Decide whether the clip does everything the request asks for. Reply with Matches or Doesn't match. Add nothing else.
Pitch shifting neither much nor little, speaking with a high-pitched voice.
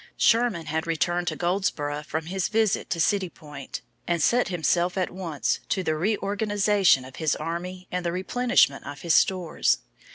Doesn't match